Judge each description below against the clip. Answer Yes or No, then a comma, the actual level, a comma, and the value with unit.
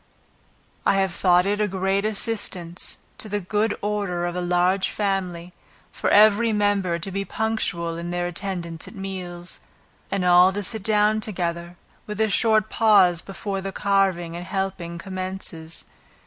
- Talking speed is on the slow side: No, average, 155 wpm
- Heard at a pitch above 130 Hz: Yes, high, 190 Hz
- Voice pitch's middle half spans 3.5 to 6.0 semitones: No, average, 2.7 semitones